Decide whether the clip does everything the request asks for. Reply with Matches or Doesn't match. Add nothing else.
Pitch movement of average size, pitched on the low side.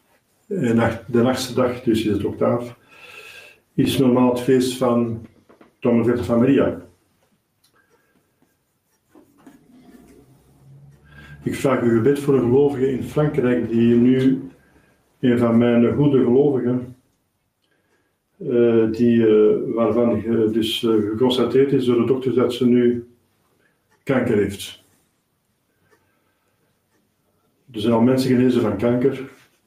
Doesn't match